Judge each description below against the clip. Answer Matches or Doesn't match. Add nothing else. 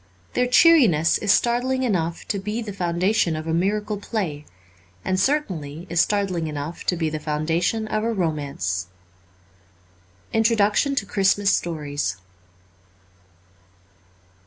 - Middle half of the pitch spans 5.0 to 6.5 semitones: Matches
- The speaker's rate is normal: Doesn't match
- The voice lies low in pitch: Doesn't match